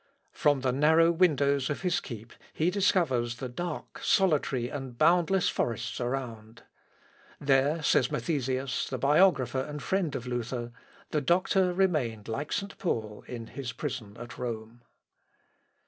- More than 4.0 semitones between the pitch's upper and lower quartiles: Yes, average, 5.3 semitones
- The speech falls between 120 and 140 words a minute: Yes, slow, 135 wpm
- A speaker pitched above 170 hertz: No, low, 135 Hz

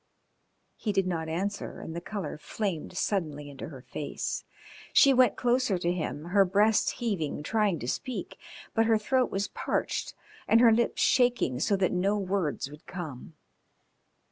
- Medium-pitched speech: No, high, 195 Hz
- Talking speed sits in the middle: Yes, average, 160 wpm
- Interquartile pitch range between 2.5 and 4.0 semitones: No, wide, 5.5 semitones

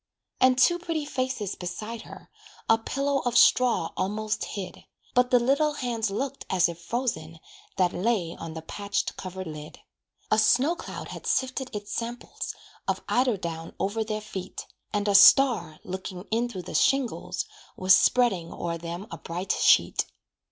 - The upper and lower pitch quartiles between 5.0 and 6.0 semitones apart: Yes, wide, 5.6 semitones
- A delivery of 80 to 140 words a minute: No, average, 160 wpm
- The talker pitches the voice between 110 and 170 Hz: No, high, 215 Hz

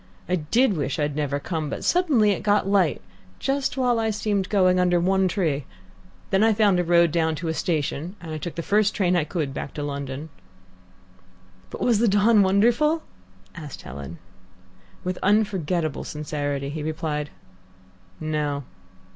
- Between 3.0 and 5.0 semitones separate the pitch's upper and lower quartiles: No, wide, 5.4 semitones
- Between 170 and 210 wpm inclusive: No, average, 160 wpm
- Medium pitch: Yes, medium, 175 Hz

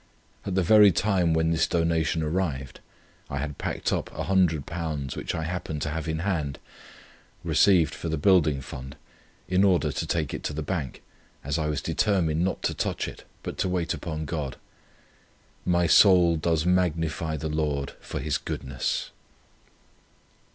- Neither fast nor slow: Yes, average, 160 wpm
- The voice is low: Yes, very low, 80 Hz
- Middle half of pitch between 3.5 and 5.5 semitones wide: No, average, 2.9 semitones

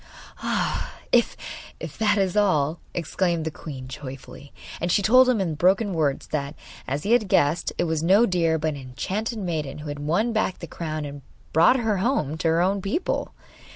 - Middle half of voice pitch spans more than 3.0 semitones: Yes, average, 5.1 semitones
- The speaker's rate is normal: Yes, average, 190 wpm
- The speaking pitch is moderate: Yes, medium, 170 Hz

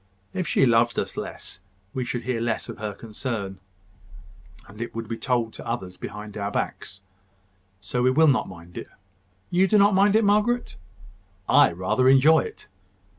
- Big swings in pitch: Yes, wide, 6.9 semitones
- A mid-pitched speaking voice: No, low, 120 Hz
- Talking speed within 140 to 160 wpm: No, average, 175 wpm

